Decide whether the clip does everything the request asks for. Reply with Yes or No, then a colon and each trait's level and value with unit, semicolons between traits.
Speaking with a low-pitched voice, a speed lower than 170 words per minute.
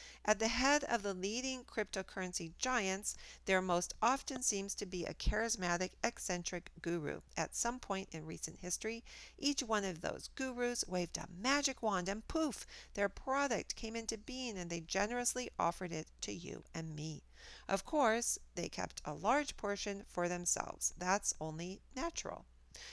No: high, 200 Hz; average, 160 wpm